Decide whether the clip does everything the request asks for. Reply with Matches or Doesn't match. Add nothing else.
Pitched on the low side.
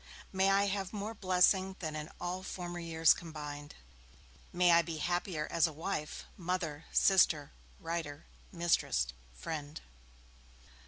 Doesn't match